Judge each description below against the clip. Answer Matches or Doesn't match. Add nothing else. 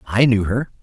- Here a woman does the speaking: Doesn't match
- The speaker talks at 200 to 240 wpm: Matches